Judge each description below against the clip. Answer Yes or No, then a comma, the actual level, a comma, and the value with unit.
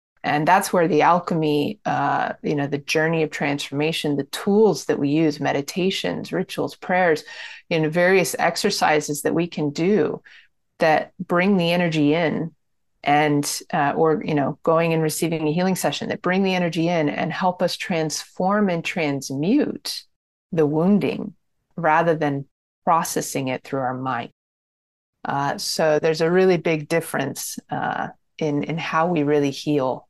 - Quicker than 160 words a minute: No, average, 155 wpm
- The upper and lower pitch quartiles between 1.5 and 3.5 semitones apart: Yes, average, 3.2 semitones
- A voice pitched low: No, medium, 160 Hz